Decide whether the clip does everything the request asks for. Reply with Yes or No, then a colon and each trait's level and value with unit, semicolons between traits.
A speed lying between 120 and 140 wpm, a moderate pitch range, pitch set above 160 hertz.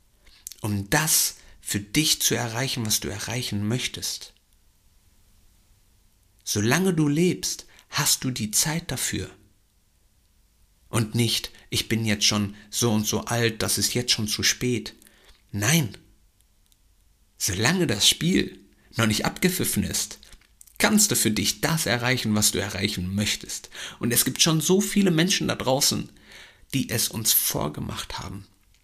No: average, 135 wpm; average, 3.5 semitones; low, 105 Hz